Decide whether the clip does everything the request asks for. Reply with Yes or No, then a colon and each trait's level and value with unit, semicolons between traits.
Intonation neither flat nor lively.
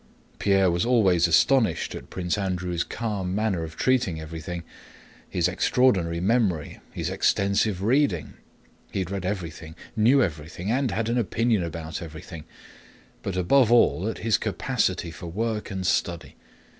Yes: average, 4.7 semitones